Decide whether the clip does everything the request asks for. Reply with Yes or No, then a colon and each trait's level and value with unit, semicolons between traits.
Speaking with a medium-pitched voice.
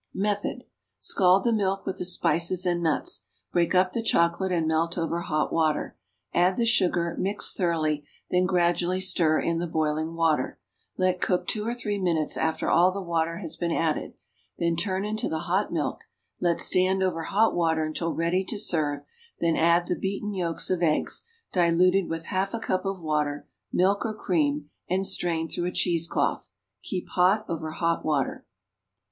Yes: medium, 175 Hz